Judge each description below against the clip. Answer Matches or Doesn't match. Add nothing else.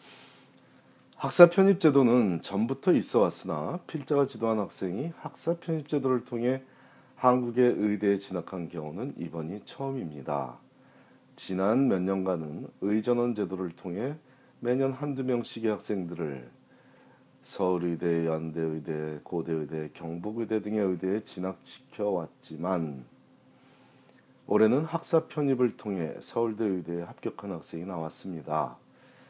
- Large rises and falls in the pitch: Matches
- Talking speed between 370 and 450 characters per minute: Doesn't match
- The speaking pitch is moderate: Doesn't match